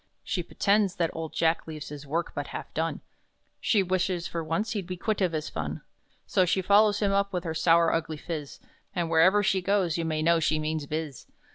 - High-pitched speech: No, medium, 170 Hz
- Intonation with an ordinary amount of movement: Yes, average, 3.3 semitones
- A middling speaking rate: No, fast, 215 wpm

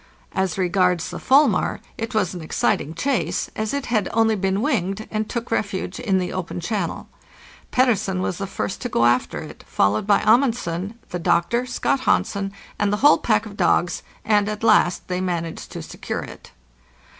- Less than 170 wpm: No, average, 180 wpm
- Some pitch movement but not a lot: Yes, average, 3.9 semitones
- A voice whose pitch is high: Yes, high, 200 Hz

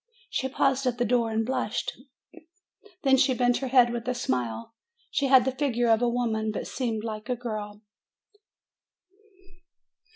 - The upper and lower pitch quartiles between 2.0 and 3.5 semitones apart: Yes, average, 2.8 semitones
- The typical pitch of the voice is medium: No, high, 240 Hz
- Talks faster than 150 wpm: Yes, average, 160 wpm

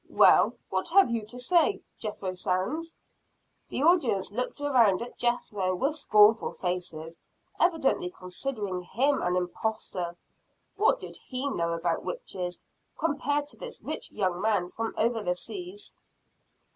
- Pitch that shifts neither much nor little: No, wide, 7.9 semitones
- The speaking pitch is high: Yes, high, 220 Hz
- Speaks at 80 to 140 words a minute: Yes, slow, 135 wpm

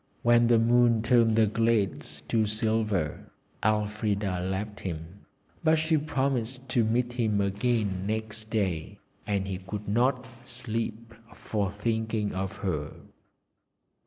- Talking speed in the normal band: No, slow, 125 wpm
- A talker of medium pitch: No, low, 110 Hz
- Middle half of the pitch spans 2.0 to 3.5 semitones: Yes, average, 2.8 semitones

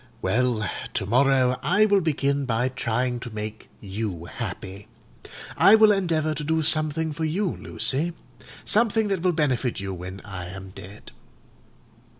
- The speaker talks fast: No, average, 150 wpm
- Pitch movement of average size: No, wide, 7.3 semitones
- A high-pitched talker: No, low, 130 Hz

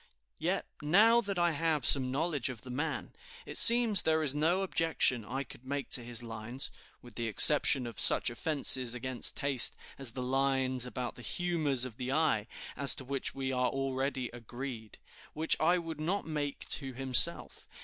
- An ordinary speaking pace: Yes, average, 180 wpm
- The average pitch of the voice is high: No, low, 135 Hz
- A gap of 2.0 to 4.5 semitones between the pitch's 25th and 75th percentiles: Yes, average, 4.0 semitones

